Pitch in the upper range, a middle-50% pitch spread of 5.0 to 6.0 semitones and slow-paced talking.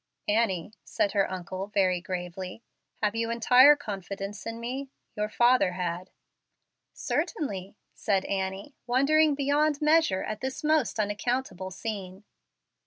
Yes: high, 210 Hz; wide, 5.5 semitones; slow, 120 wpm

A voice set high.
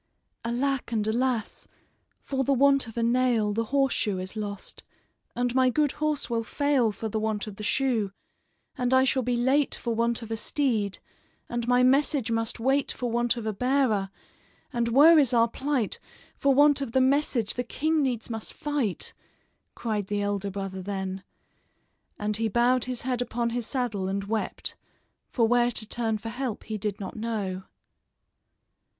Yes: high, 235 Hz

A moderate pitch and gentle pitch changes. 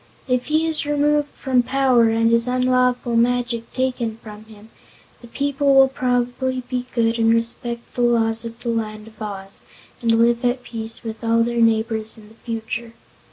No: high, 235 Hz; narrow, 2.0 semitones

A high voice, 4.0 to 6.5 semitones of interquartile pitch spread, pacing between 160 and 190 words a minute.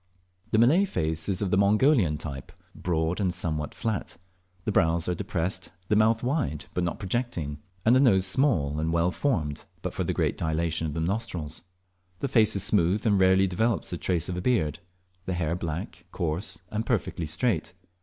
No: very low, 90 Hz; average, 5.1 semitones; average, 185 wpm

